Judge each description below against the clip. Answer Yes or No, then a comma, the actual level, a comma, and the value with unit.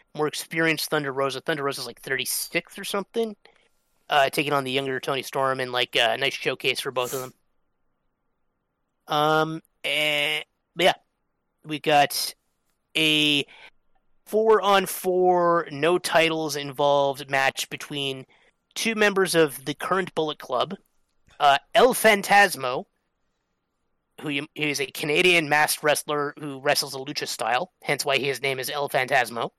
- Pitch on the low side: No, medium, 150 Hz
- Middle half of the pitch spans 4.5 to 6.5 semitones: No, average, 3.8 semitones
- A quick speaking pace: No, average, 145 wpm